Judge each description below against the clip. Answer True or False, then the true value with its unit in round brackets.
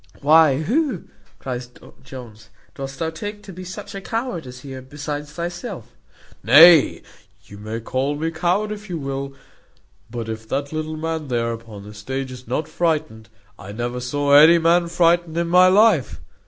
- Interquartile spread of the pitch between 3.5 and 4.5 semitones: False (5.4 semitones)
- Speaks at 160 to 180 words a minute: True (165 wpm)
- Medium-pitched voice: True (145 Hz)